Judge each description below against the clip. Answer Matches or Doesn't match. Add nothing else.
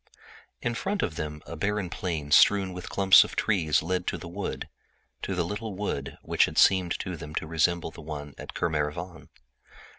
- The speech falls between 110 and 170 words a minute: Doesn't match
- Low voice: Matches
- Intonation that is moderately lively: Matches